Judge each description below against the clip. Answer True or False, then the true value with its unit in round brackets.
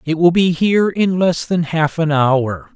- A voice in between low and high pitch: True (165 Hz)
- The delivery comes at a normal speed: False (220 wpm)